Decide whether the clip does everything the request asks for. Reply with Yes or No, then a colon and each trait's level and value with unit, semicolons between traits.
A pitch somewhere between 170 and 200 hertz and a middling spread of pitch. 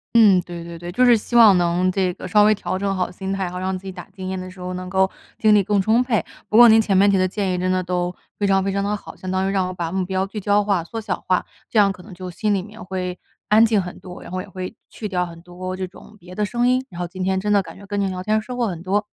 No: high, 190 Hz; narrow, 2.3 semitones